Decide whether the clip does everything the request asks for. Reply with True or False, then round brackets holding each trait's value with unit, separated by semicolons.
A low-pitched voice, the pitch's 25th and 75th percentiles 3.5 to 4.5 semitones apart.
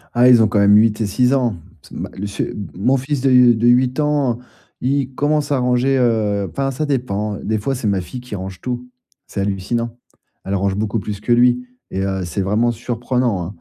True (120 Hz; 3.8 semitones)